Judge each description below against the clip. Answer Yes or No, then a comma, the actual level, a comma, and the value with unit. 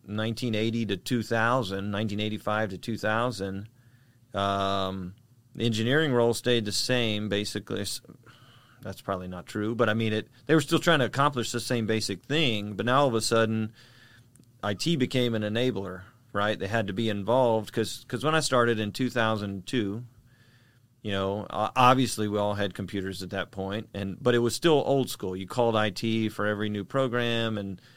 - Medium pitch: No, low, 115 Hz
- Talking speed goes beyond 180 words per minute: No, average, 175 wpm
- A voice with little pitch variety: No, average, 3.0 semitones